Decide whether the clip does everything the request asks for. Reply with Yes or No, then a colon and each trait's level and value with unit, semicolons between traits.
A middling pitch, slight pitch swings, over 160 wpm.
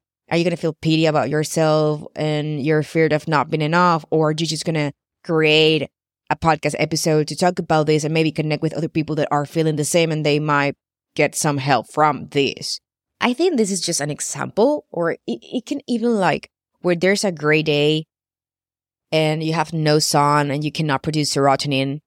Yes: medium, 155 Hz; narrow, 1.6 semitones; average, 200 wpm